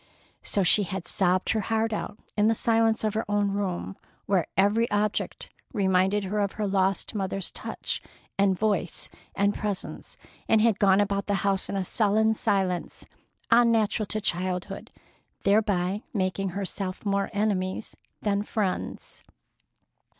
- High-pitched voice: Yes, high, 200 Hz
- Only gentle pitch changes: Yes, narrow, 1.9 semitones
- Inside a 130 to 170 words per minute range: Yes, average, 145 wpm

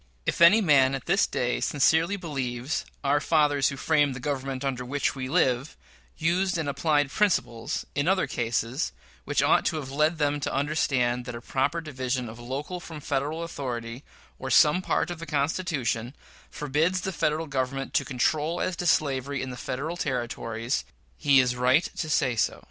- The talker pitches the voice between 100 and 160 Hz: Yes, medium, 140 Hz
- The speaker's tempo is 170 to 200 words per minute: Yes, average, 175 wpm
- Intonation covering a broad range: No, average, 3.8 semitones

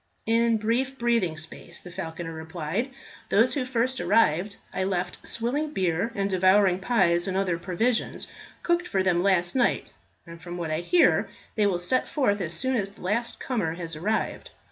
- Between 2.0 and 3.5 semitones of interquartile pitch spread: No, average, 5.2 semitones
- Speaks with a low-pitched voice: No, high, 195 Hz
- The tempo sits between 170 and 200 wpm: Yes, average, 175 wpm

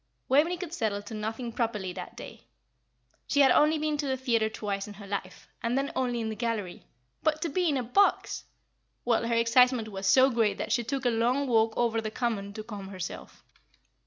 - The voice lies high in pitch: Yes, high, 235 Hz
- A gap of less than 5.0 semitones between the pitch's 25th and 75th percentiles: Yes, average, 3.5 semitones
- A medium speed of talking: No, fast, 210 wpm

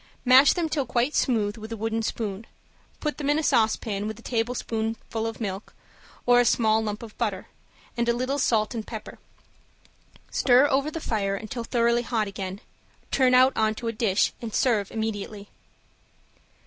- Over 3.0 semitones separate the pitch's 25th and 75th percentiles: No, narrow, 2.6 semitones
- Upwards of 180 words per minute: No, average, 175 wpm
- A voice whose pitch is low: No, high, 225 Hz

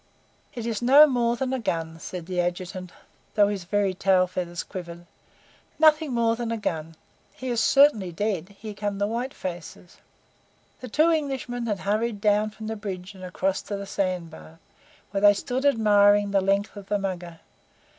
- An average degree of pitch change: Yes, average, 4.1 semitones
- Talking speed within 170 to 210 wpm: Yes, average, 180 wpm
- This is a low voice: No, high, 205 Hz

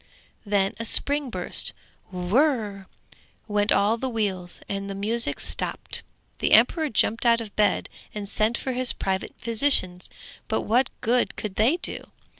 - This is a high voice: Yes, high, 220 Hz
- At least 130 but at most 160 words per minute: Yes, average, 150 wpm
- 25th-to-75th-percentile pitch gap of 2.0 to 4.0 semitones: Yes, average, 3.6 semitones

